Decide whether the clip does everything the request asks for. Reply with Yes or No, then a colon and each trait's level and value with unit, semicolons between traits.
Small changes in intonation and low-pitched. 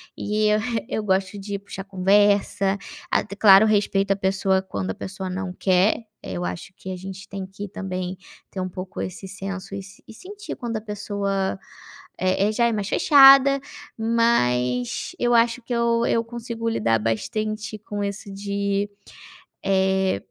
No: narrow, 2.3 semitones; high, 200 Hz